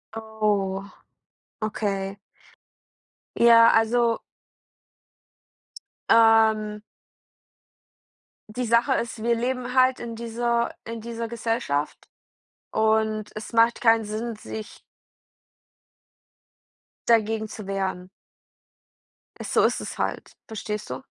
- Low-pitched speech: No, high, 225 Hz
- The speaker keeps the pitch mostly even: Yes, narrow, 1.7 semitones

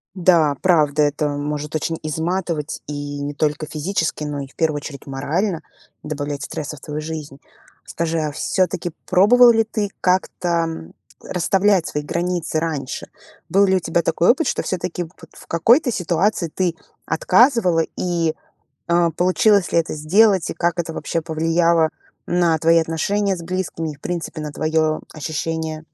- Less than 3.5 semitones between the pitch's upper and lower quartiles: Yes, average, 3.0 semitones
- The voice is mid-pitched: Yes, medium, 165 Hz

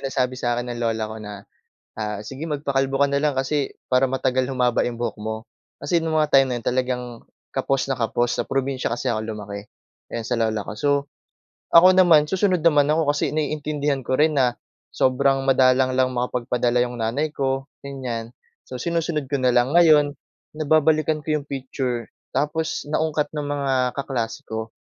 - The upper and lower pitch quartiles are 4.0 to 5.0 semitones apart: No, average, 3.4 semitones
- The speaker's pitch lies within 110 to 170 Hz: Yes, low, 135 Hz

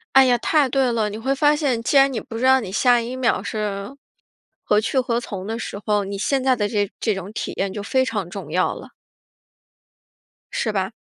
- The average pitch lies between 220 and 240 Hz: Yes, high, 230 Hz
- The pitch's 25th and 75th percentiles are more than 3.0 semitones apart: Yes, average, 4.1 semitones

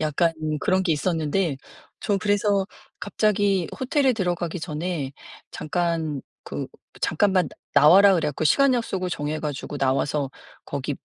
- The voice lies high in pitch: No, medium, 175 Hz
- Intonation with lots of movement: No, average, 4.8 semitones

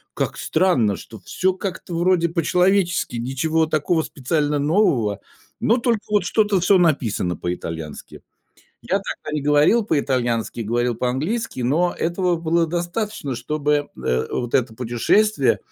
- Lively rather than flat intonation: Yes, wide, 6.7 semitones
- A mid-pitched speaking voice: Yes, medium, 155 Hz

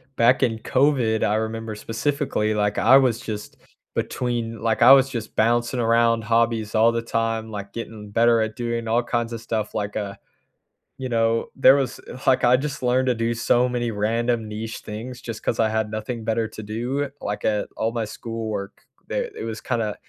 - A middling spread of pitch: No, narrow, 1.7 semitones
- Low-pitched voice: Yes, low, 115 Hz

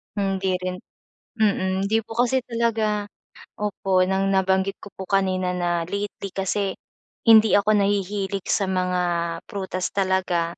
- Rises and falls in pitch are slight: Yes, narrow, 1.7 semitones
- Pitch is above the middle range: Yes, high, 195 Hz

